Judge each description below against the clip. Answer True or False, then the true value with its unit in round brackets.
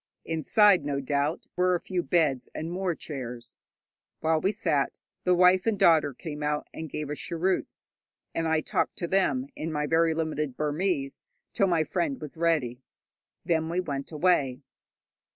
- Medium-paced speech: True (165 wpm)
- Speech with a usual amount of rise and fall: True (3.5 semitones)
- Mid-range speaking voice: True (160 Hz)